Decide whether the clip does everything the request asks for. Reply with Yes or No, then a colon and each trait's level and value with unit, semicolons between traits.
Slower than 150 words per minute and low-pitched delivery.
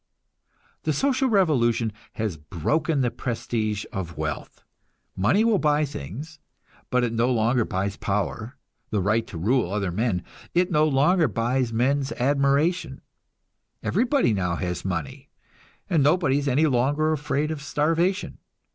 Yes: average, 140 wpm; low, 130 Hz